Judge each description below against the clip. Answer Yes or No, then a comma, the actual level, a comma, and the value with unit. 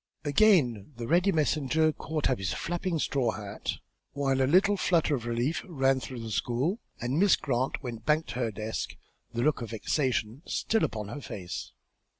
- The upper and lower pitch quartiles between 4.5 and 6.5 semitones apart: Yes, average, 5.3 semitones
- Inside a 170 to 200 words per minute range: Yes, average, 175 wpm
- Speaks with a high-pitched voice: No, low, 135 Hz